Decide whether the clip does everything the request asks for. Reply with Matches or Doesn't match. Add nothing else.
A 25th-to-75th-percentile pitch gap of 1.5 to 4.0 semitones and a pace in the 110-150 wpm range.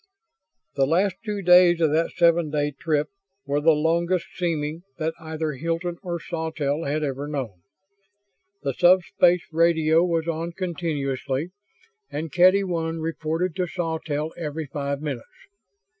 Matches